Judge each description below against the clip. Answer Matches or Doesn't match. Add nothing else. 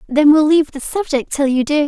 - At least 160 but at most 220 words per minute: Doesn't match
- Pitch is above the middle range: Matches